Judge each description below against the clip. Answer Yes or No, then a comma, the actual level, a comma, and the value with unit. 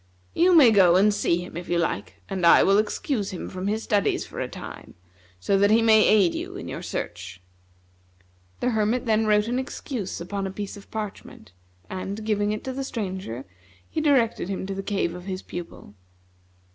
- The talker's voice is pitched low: No, high, 205 Hz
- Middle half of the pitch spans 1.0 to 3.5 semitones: Yes, average, 2.9 semitones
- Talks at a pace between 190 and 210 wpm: Yes, average, 195 wpm